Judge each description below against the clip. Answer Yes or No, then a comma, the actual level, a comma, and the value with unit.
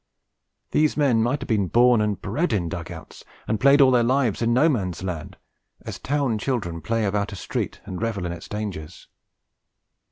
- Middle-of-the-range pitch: No, low, 110 Hz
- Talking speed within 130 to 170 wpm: No, average, 190 wpm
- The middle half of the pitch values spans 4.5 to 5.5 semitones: Yes, average, 5.2 semitones